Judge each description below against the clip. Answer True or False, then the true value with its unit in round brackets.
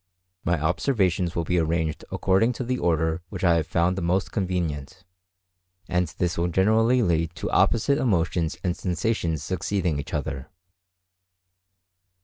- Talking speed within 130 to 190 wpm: True (140 wpm)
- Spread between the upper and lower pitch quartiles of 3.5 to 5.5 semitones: False (2.9 semitones)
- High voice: False (90 Hz)